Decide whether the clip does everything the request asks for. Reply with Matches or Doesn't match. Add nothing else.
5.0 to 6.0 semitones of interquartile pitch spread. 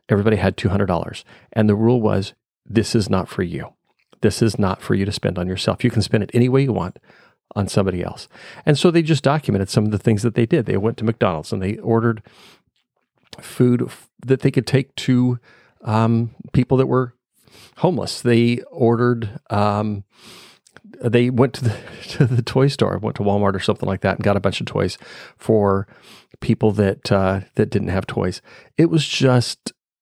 Doesn't match